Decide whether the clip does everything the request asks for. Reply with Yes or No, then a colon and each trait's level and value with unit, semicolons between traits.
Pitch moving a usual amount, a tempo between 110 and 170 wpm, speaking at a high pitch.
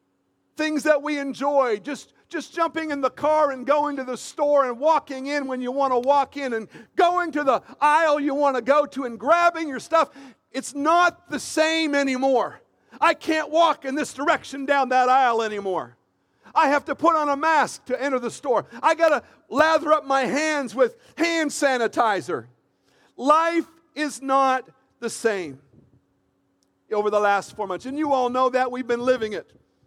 No: average, 3.7 semitones; average, 185 wpm; very high, 280 Hz